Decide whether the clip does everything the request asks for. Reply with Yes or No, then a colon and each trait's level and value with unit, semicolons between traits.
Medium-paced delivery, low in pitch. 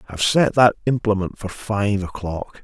Yes: average, 160 wpm; low, 105 Hz